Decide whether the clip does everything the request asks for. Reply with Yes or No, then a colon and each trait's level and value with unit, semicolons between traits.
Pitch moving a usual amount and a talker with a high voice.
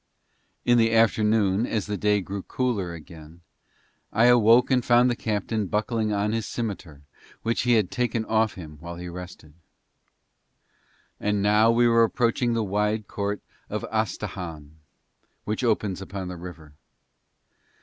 No: average, 3.6 semitones; low, 105 Hz